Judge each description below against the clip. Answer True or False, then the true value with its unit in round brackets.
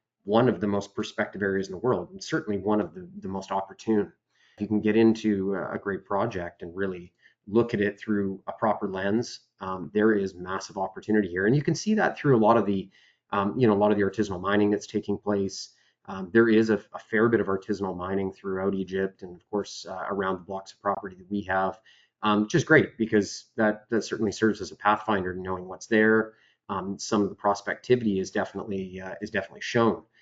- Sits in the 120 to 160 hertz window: False (100 Hz)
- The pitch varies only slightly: True (2.2 semitones)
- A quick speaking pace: True (220 wpm)